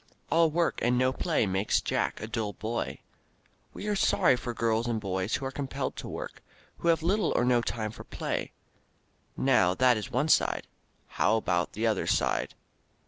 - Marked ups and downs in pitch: No, average, 3.9 semitones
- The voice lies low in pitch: Yes, low, 120 Hz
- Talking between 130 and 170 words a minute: No, average, 185 wpm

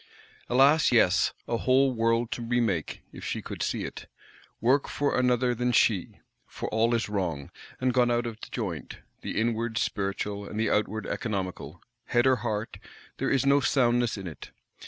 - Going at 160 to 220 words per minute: Yes, average, 170 wpm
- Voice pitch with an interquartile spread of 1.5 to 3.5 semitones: Yes, average, 2.8 semitones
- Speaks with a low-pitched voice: Yes, low, 115 Hz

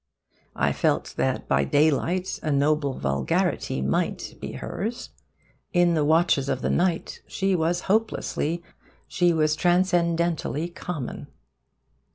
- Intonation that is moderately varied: Yes, average, 3.3 semitones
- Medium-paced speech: No, slow, 120 wpm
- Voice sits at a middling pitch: Yes, medium, 170 Hz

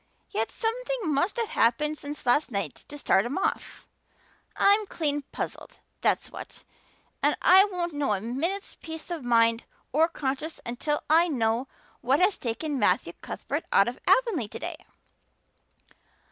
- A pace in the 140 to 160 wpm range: Yes, average, 145 wpm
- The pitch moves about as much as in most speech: No, wide, 6.7 semitones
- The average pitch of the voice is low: No, very high, 295 Hz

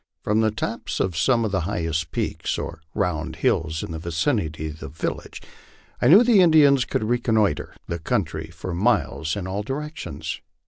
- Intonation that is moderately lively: No, wide, 6.7 semitones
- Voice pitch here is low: Yes, very low, 95 Hz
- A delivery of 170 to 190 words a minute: Yes, average, 175 wpm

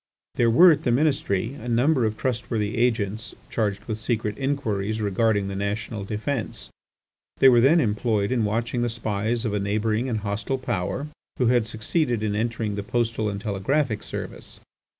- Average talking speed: Yes, average, 170 wpm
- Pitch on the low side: Yes, low, 110 Hz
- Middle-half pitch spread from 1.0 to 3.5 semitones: Yes, average, 2.8 semitones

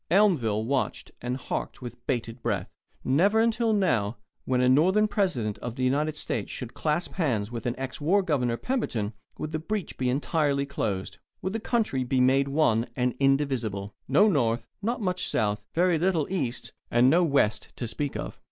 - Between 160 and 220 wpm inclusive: Yes, average, 175 wpm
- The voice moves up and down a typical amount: No, wide, 6.7 semitones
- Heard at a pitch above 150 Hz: No, low, 135 Hz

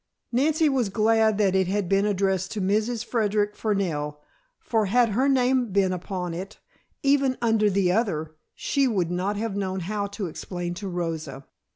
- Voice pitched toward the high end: Yes, high, 200 Hz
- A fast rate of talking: No, average, 170 wpm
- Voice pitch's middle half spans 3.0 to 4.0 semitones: Yes, average, 3.5 semitones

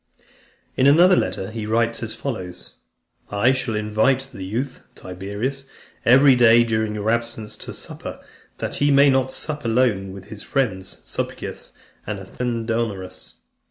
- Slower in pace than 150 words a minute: Yes, average, 140 wpm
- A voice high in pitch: No, low, 115 Hz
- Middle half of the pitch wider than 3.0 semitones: Yes, average, 3.8 semitones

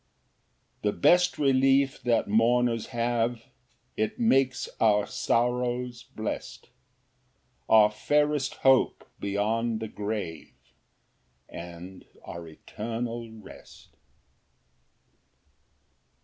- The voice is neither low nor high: No, low, 115 Hz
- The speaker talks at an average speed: No, slow, 80 wpm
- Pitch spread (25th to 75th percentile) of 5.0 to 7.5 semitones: No, average, 2.9 semitones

